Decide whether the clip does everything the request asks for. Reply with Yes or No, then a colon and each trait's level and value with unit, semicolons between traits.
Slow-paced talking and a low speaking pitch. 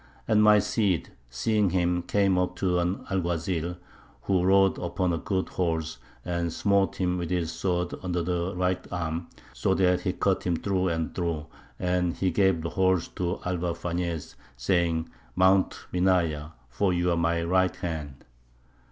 No: average, 160 wpm; very low, 90 Hz